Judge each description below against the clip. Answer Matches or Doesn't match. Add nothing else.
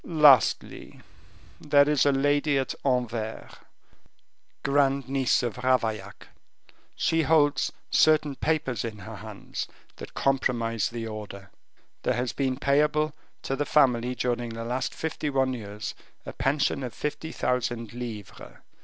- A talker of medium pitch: Doesn't match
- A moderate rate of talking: Doesn't match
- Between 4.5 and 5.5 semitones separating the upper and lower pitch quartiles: Doesn't match